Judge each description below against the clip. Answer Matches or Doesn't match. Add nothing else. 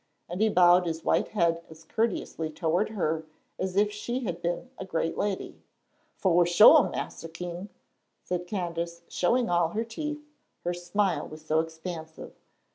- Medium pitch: Matches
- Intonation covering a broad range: Doesn't match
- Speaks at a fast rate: Doesn't match